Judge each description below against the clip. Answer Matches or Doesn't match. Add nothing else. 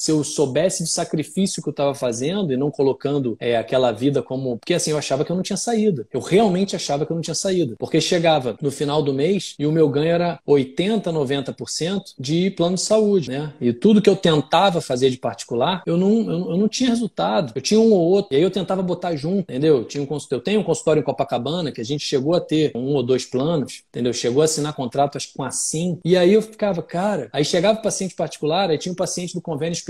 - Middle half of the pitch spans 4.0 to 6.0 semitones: Matches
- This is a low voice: Doesn't match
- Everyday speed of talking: Doesn't match